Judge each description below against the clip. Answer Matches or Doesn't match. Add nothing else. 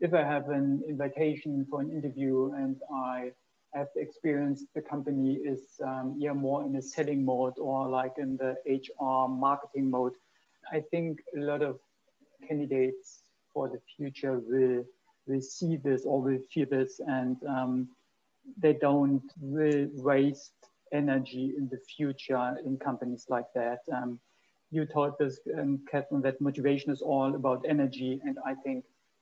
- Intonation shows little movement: Matches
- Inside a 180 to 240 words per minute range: Doesn't match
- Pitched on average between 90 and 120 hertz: Doesn't match